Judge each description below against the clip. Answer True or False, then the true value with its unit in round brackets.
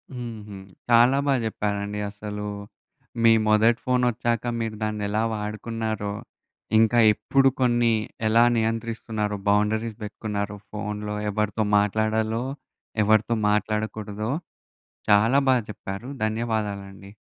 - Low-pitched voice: True (110 Hz)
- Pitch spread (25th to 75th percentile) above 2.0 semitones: False (1.7 semitones)